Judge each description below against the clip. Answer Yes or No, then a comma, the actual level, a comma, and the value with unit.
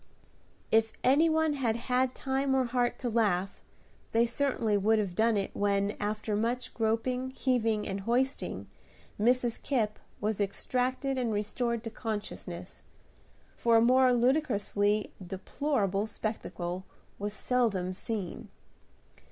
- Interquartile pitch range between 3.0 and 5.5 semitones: Yes, average, 3.6 semitones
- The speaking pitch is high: Yes, high, 225 Hz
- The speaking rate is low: Yes, slow, 125 wpm